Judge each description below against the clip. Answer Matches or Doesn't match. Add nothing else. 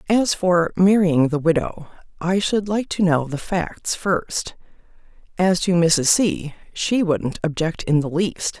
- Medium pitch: Matches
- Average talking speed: Matches